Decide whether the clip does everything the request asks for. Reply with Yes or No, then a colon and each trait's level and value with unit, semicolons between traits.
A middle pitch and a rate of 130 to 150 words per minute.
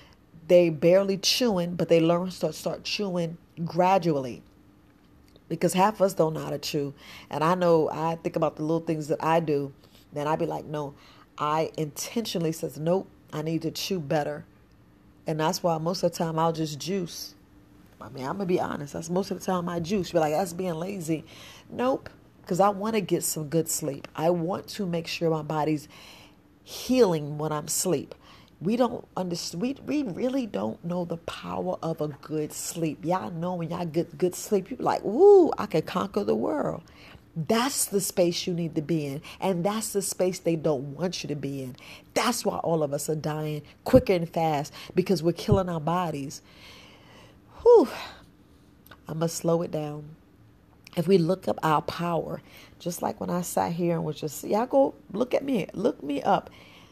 No: medium, 170 Hz; average, 200 wpm